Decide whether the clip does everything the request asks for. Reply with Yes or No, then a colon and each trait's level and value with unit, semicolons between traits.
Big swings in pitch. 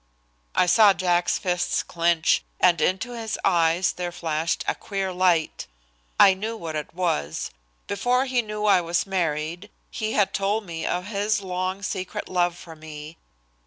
No: average, 3.1 semitones